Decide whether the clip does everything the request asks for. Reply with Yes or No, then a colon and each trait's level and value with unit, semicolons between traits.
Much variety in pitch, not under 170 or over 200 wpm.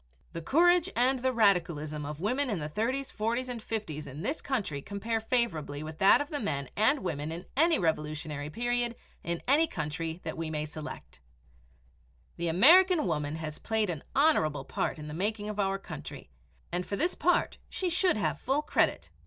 Yes: wide, 8.6 semitones; average, 185 wpm